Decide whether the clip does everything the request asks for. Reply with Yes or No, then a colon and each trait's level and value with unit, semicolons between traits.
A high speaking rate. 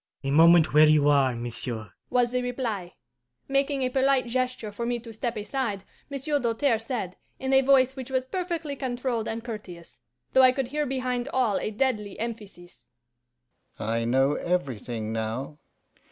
No: average, 160 wpm